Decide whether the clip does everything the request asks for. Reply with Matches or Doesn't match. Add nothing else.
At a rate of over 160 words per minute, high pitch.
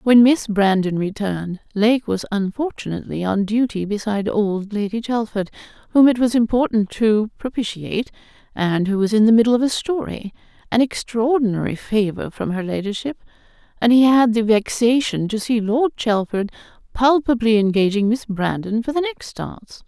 Doesn't match